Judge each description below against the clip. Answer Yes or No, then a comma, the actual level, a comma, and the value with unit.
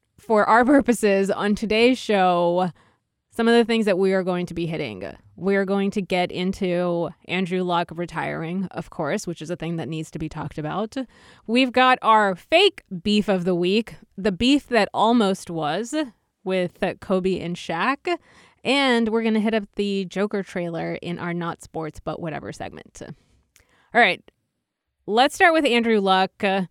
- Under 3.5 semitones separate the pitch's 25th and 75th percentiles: No, average, 4.2 semitones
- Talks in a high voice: Yes, high, 195 Hz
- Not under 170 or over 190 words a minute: Yes, average, 175 wpm